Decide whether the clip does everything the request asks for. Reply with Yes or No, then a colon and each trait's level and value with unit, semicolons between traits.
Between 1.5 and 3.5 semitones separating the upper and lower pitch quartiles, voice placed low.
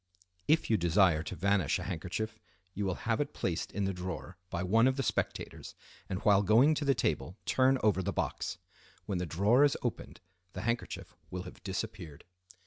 No: average, 4.1 semitones; low, 100 Hz